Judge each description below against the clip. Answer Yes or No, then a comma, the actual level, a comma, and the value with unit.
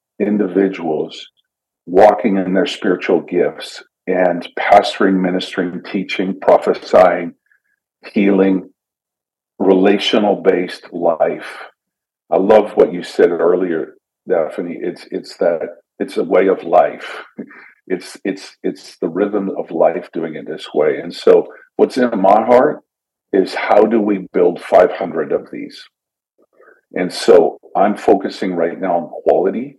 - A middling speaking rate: No, slow, 125 wpm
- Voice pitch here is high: No, low, 105 Hz